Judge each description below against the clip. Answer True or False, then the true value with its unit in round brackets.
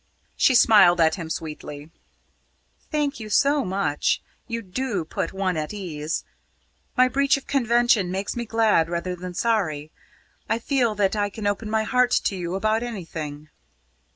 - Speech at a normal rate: True (155 wpm)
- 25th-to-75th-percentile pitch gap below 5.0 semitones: False (5.4 semitones)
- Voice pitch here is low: False (205 Hz)